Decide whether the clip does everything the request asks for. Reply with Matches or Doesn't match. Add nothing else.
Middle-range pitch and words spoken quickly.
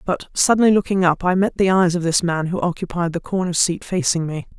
Matches